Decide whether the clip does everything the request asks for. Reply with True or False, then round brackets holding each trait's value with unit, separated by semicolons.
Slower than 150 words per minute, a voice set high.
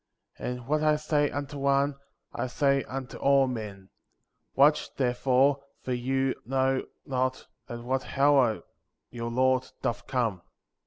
False (135 wpm; 130 Hz)